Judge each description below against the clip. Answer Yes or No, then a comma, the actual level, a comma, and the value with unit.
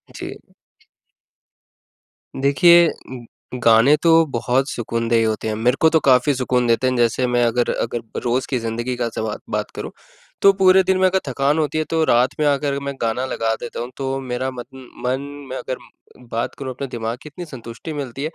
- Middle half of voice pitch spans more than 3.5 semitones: No, average, 3.1 semitones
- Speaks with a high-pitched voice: No, low, 130 Hz